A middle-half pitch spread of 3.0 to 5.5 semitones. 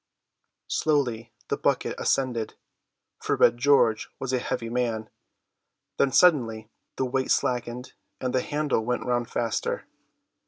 No: narrow, 2.4 semitones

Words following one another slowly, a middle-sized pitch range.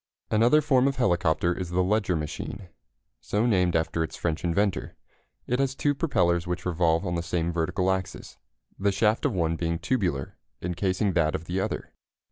No: average, 175 wpm; average, 3.9 semitones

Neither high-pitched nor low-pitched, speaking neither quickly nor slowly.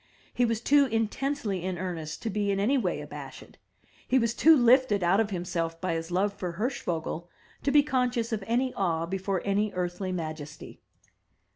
No: high, 200 Hz; average, 175 wpm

